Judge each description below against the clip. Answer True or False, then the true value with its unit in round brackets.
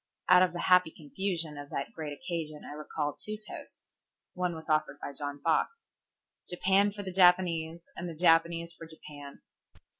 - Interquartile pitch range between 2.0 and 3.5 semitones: True (2.9 semitones)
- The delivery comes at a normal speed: True (170 wpm)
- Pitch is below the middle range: False (165 Hz)